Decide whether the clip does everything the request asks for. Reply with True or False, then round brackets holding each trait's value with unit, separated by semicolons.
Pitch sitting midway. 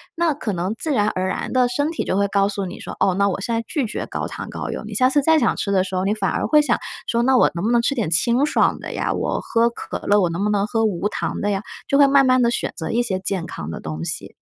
False (215 Hz)